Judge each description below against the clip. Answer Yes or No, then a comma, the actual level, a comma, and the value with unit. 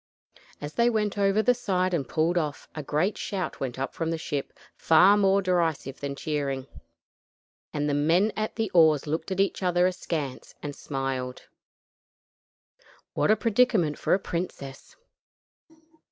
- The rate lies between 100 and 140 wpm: No, average, 155 wpm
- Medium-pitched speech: Yes, medium, 170 Hz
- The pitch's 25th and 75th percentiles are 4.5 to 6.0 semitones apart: Yes, average, 5.2 semitones